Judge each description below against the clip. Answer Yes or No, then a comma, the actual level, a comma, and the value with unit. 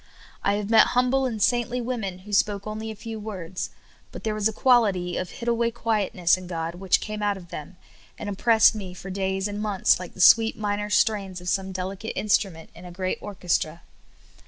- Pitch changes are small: No, average, 3.1 semitones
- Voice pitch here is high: Yes, high, 205 Hz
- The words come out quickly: Yes, fast, 210 wpm